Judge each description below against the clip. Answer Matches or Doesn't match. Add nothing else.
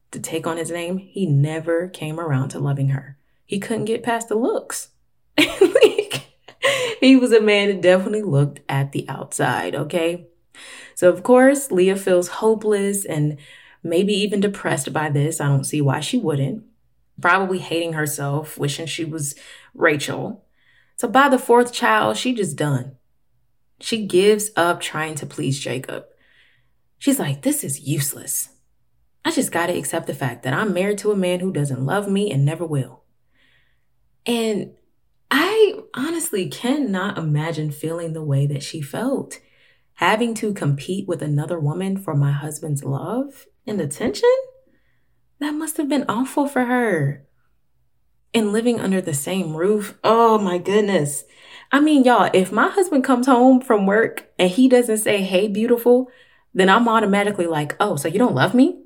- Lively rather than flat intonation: Matches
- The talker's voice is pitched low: Doesn't match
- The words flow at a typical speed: Matches